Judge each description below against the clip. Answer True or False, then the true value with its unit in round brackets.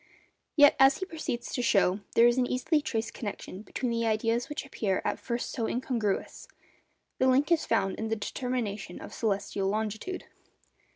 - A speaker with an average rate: True (175 wpm)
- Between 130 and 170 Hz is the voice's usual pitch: False (235 Hz)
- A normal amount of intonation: True (3.4 semitones)